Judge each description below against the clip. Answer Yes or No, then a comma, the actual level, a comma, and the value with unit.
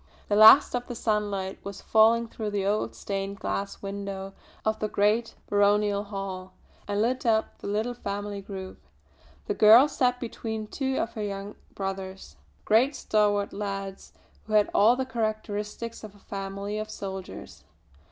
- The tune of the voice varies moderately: No, narrow, 1.9 semitones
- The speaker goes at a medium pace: Yes, average, 155 wpm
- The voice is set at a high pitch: Yes, high, 210 Hz